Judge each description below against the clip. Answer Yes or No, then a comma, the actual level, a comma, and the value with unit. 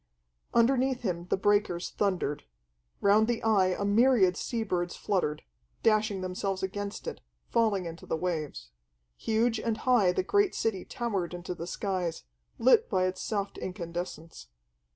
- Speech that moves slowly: No, average, 145 wpm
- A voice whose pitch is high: Yes, high, 195 Hz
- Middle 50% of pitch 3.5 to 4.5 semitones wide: Yes, average, 3.8 semitones